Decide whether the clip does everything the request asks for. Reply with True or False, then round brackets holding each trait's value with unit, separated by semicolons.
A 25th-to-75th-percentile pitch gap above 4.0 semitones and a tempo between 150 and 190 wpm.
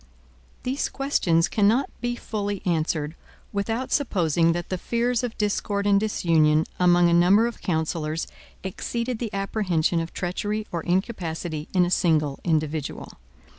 False (4.8 semitones; 135 wpm)